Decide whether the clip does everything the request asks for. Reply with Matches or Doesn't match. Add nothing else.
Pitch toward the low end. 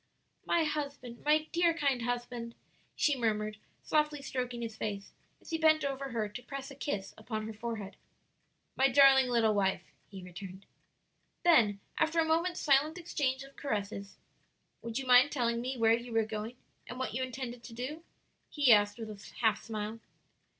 Doesn't match